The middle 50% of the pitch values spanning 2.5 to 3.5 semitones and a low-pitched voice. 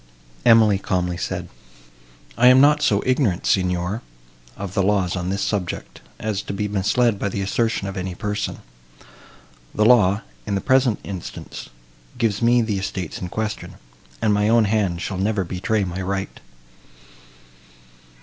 Yes: average, 2.8 semitones; low, 100 Hz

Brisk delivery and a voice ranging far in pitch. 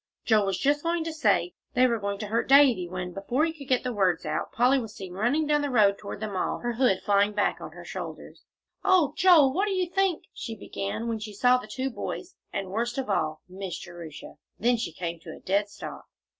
Yes: fast, 240 wpm; wide, 5.8 semitones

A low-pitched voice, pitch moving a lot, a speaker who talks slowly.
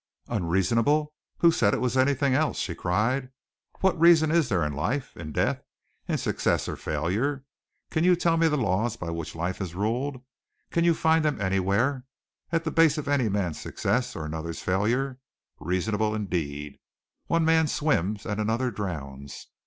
No: low, 115 Hz; wide, 8.1 semitones; average, 170 wpm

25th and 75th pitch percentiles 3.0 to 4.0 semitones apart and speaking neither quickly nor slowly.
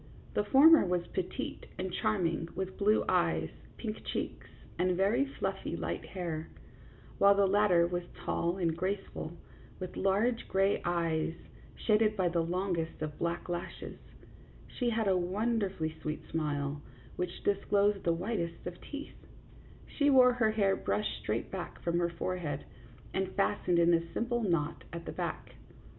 Yes: average, 3.6 semitones; average, 150 wpm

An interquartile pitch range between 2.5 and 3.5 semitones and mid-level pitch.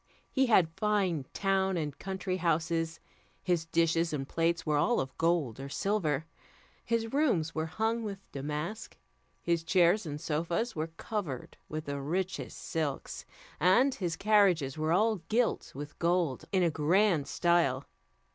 No: average, 4.1 semitones; medium, 170 Hz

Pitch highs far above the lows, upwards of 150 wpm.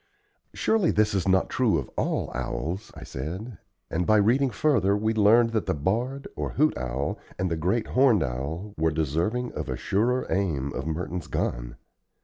Yes: wide, 6.5 semitones; average, 175 wpm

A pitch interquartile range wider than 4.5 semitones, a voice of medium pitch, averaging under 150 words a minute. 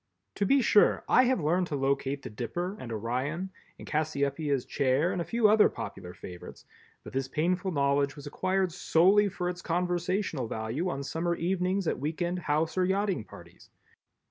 No: average, 4.9 semitones; medium, 165 Hz; average, 175 wpm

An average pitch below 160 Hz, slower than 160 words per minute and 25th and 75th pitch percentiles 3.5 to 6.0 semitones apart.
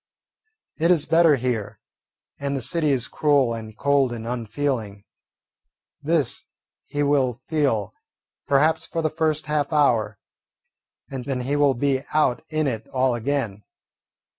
Yes: low, 135 Hz; average, 140 wpm; average, 3.9 semitones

